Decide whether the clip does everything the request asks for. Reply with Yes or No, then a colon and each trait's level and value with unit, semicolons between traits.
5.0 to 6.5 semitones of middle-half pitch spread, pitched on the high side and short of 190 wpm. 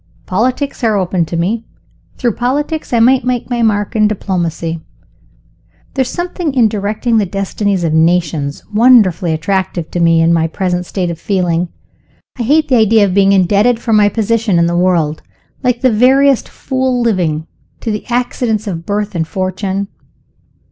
Yes: average, 5.3 semitones; high, 205 Hz; average, 170 wpm